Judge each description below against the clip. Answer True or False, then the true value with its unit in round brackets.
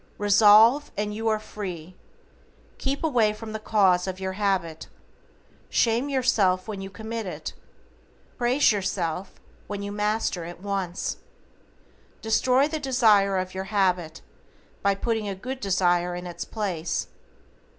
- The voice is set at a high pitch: True (205 Hz)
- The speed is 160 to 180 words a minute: False (135 wpm)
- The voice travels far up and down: False (3.3 semitones)